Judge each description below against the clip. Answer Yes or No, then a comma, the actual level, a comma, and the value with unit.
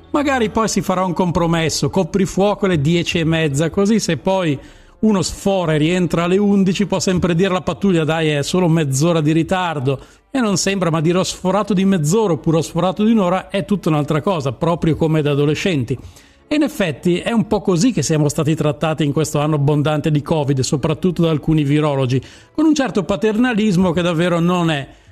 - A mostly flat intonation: No, average, 4.0 semitones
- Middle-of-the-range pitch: Yes, medium, 170 Hz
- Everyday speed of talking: No, fast, 200 wpm